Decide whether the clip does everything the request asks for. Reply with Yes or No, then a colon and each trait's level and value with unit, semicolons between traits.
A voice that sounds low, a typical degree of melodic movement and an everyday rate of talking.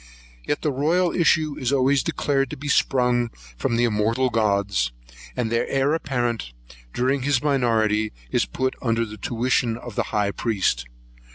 Yes: low, 120 Hz; average, 3.7 semitones; average, 160 wpm